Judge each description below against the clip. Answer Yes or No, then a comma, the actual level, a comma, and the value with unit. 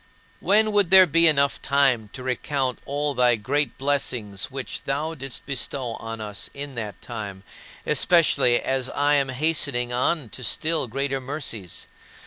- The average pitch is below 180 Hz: Yes, low, 135 Hz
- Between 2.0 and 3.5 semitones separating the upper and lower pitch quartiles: Yes, average, 3.2 semitones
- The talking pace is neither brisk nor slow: Yes, average, 150 wpm